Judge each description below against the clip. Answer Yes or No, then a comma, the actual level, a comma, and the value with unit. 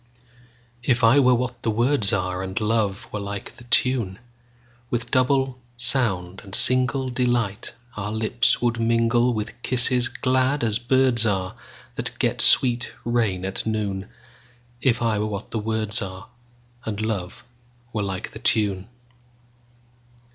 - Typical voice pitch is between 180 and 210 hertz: No, low, 115 Hz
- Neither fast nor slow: No, slow, 120 wpm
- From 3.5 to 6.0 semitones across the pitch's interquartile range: No, average, 2.8 semitones